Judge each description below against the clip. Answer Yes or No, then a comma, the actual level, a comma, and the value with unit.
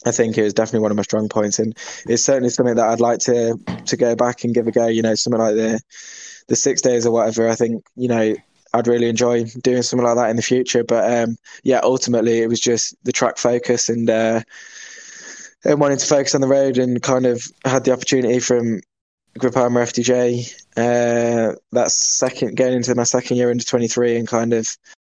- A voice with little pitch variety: Yes, narrow, 1.6 semitones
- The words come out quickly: Yes, fast, 215 wpm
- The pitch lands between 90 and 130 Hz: Yes, low, 120 Hz